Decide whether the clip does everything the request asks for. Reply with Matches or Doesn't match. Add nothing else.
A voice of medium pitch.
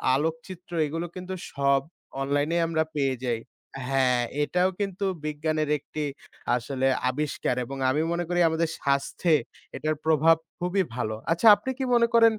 Matches